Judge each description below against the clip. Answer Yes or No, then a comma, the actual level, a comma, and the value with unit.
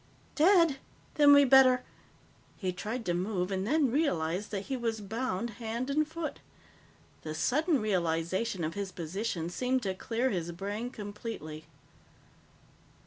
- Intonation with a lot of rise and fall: Yes, wide, 6.1 semitones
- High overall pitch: Yes, high, 220 Hz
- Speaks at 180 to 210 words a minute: No, average, 140 wpm